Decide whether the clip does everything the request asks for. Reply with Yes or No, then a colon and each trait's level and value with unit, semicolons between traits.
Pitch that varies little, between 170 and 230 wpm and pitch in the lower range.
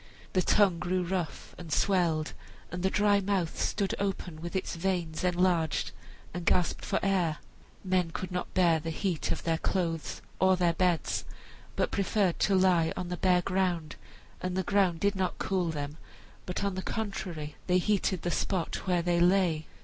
No: narrow, 2.2 semitones; average, 180 wpm; medium, 180 Hz